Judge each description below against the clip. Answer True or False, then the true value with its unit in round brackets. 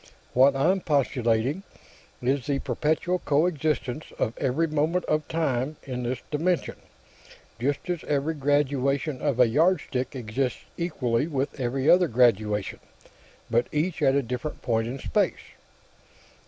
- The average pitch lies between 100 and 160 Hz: True (140 Hz)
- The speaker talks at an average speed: False (130 wpm)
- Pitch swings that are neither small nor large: True (3.7 semitones)